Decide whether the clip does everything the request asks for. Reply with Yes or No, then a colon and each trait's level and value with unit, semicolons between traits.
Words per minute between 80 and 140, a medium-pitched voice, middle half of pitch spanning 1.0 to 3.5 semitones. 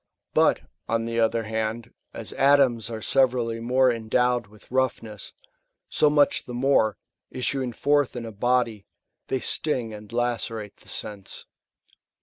No: slow, 135 wpm; low, 120 Hz; narrow, 2.5 semitones